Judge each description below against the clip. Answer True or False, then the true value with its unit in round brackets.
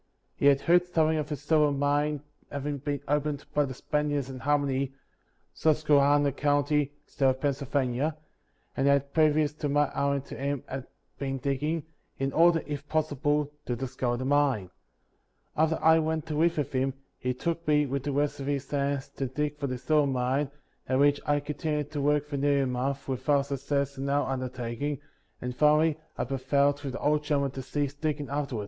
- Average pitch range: False (1.6 semitones)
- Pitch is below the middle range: False (145 Hz)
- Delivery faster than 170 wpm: True (190 wpm)